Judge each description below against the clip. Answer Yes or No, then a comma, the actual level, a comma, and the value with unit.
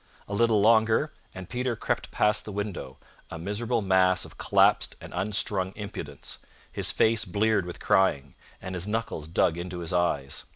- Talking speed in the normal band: Yes, average, 165 wpm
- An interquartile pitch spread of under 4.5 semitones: Yes, average, 3.9 semitones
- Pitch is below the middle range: Yes, very low, 95 Hz